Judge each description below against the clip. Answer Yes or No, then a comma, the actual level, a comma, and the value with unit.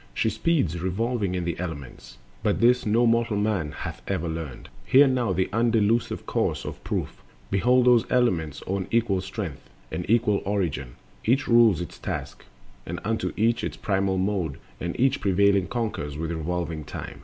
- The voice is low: Yes, low, 100 Hz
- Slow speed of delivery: No, average, 165 wpm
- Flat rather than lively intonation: No, average, 5.1 semitones